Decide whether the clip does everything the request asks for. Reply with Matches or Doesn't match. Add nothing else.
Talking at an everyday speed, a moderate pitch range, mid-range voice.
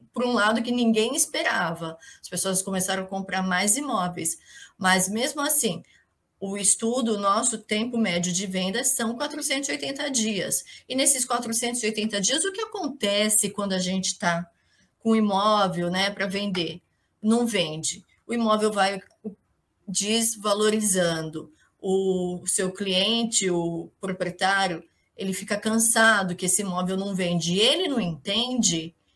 Doesn't match